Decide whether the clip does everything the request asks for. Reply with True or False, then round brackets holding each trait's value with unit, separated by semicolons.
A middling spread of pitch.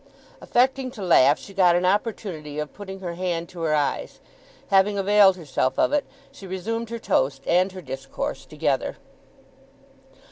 True (4.0 semitones)